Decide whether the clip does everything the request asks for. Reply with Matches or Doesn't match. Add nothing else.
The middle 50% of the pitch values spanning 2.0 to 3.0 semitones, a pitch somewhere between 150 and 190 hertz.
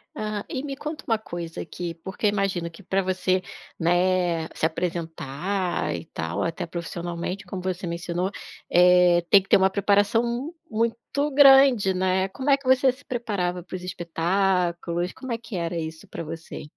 Doesn't match